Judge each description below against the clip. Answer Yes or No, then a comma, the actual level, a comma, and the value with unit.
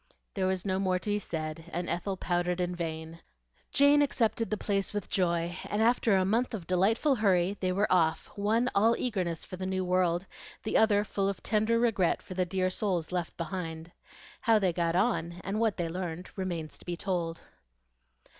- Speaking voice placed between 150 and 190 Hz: Yes, medium, 185 Hz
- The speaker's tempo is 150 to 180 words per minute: No, average, 190 wpm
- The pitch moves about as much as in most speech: Yes, average, 3.1 semitones